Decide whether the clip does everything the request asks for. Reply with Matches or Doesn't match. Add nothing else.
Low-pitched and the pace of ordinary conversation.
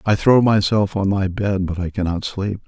Doesn't match